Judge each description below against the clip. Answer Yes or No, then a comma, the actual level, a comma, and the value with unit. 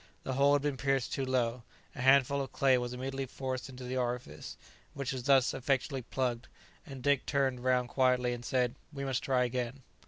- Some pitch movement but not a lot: No, narrow, 1.6 semitones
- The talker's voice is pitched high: No, low, 130 Hz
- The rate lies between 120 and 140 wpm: No, average, 195 wpm